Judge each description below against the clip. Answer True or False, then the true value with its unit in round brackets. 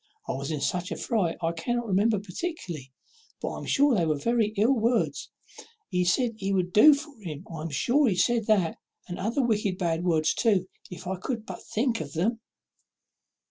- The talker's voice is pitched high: True (195 Hz)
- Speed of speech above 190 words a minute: True (200 wpm)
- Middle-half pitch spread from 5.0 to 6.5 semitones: True (5.4 semitones)